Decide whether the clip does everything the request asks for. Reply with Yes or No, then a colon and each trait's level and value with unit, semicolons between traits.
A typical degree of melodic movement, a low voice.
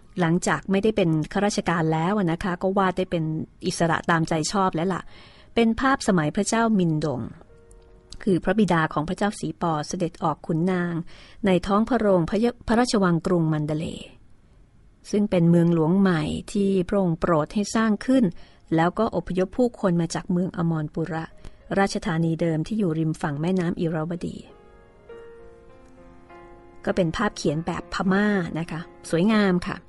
No: average, 3.8 semitones; medium, 180 Hz